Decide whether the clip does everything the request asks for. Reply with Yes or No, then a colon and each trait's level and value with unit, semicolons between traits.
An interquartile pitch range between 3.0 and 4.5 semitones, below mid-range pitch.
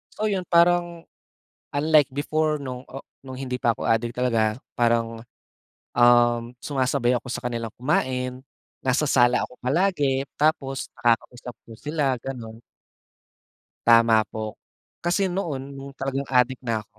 Yes: average, 3.4 semitones; low, 130 Hz